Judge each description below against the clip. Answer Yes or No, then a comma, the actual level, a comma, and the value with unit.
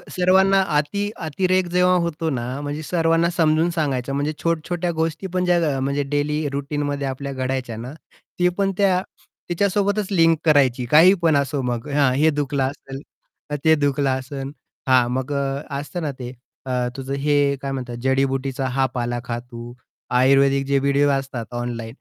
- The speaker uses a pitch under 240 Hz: Yes, medium, 140 Hz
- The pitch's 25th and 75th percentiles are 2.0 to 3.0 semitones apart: No, average, 3.7 semitones